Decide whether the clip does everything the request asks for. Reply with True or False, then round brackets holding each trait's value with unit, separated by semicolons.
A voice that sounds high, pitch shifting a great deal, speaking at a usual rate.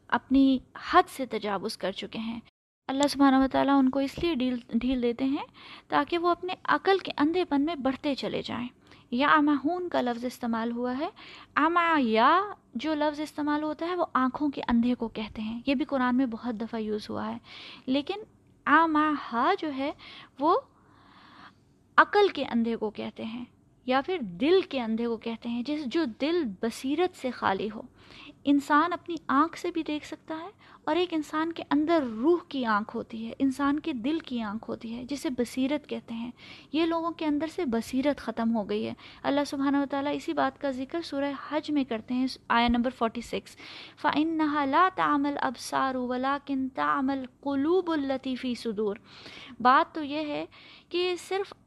False (280 Hz; 4.6 semitones; 180 wpm)